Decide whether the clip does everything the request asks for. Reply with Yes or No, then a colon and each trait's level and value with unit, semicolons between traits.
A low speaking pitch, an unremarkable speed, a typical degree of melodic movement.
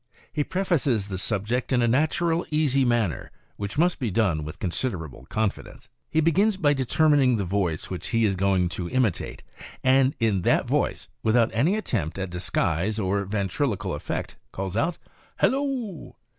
No: low, 115 Hz; average, 155 wpm; wide, 7.2 semitones